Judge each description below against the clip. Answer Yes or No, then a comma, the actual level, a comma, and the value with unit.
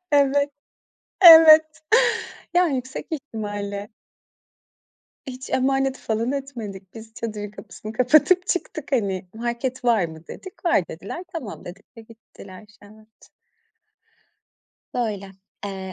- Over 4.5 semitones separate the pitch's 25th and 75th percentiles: Yes, average, 5.2 semitones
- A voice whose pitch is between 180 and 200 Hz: No, high, 230 Hz